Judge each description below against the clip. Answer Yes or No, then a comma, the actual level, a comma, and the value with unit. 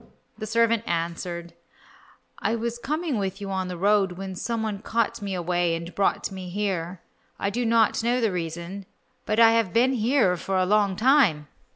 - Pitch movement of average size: Yes, average, 4.2 semitones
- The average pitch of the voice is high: Yes, high, 200 Hz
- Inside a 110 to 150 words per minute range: No, average, 185 wpm